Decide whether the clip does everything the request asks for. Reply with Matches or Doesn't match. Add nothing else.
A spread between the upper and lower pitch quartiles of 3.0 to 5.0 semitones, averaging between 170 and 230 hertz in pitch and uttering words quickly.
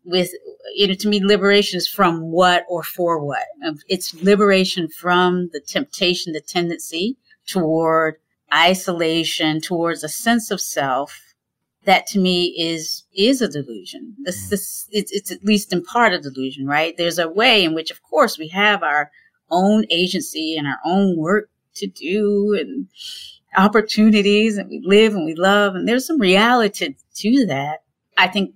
Doesn't match